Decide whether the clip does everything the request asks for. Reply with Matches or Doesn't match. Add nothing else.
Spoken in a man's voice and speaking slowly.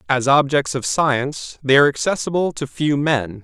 Doesn't match